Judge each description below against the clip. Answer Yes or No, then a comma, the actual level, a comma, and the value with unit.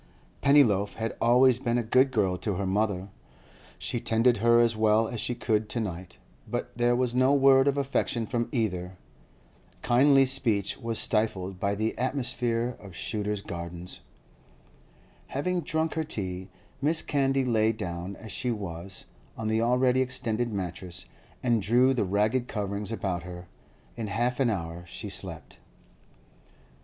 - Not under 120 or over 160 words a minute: Yes, average, 150 wpm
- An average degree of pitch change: Yes, average, 4.1 semitones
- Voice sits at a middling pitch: No, low, 115 Hz